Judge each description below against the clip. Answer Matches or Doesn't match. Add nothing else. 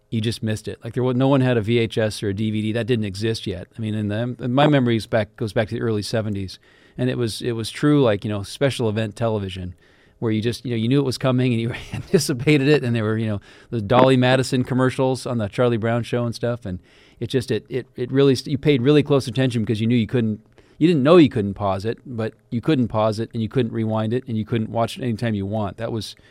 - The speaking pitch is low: Matches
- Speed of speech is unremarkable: Doesn't match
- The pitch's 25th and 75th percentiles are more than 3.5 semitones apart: Doesn't match